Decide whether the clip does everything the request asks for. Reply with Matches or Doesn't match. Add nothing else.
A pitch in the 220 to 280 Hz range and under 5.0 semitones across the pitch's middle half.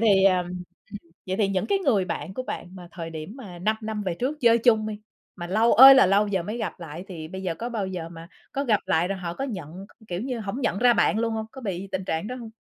Doesn't match